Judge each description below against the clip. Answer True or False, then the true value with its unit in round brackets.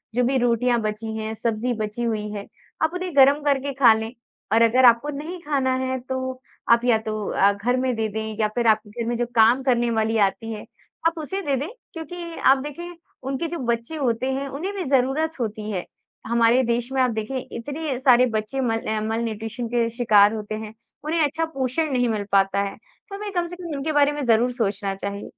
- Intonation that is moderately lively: True (4.1 semitones)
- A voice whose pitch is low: False (245 Hz)